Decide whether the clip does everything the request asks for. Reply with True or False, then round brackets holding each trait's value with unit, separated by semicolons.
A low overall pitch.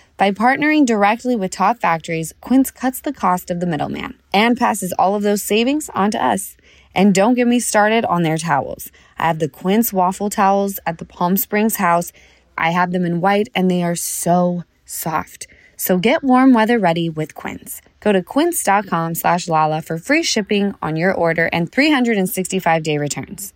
False (190 Hz)